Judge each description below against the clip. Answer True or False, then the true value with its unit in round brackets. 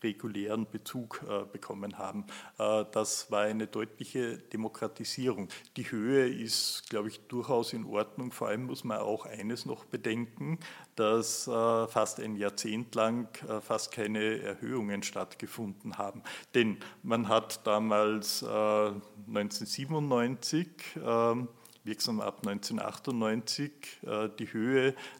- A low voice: True (110 Hz)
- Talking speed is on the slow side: True (105 wpm)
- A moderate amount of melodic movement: False (2.1 semitones)